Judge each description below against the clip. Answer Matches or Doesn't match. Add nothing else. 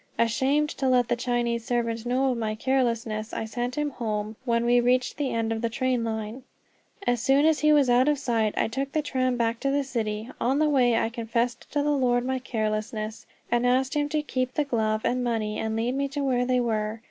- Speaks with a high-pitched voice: Matches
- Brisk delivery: Matches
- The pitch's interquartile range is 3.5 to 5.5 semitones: Doesn't match